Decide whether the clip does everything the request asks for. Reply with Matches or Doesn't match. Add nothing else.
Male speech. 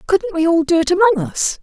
Doesn't match